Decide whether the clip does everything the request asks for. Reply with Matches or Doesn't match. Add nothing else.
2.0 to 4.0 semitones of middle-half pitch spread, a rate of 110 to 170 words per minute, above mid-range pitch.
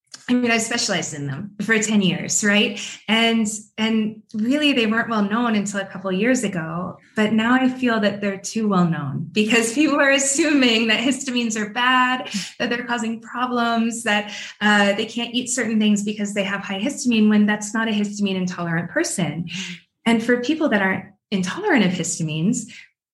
Doesn't match